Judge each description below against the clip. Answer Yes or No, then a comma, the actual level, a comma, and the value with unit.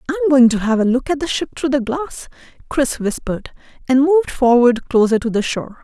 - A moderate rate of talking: No, fast, 215 wpm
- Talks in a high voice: Yes, very high, 260 Hz